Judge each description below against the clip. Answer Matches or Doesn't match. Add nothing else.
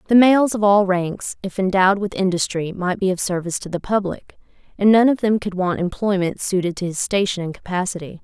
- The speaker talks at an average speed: Doesn't match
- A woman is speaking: Matches